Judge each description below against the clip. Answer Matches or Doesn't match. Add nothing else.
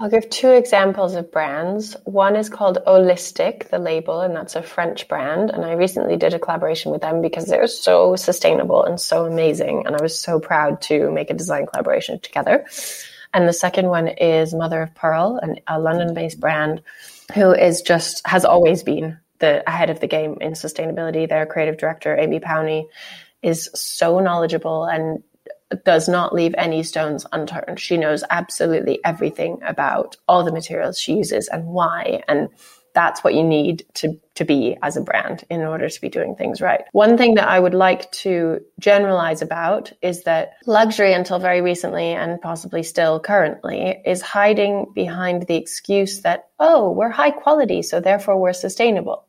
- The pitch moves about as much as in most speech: Matches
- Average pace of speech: Matches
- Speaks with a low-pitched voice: Doesn't match